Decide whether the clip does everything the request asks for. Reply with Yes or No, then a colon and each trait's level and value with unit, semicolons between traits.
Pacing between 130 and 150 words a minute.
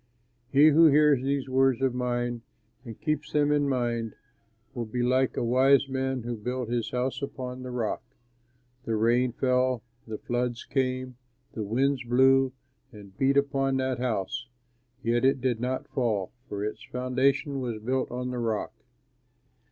No: average, 160 wpm